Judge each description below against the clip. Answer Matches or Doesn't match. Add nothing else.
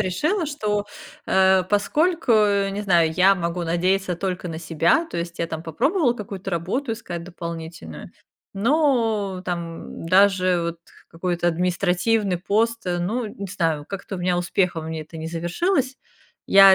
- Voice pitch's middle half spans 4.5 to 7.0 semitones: Doesn't match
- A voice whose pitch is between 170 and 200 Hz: Matches